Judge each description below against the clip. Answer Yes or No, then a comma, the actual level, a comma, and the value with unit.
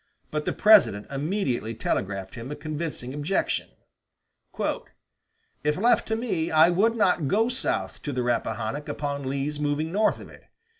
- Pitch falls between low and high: Yes, medium, 150 Hz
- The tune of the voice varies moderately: No, wide, 6.0 semitones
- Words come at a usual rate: Yes, average, 150 wpm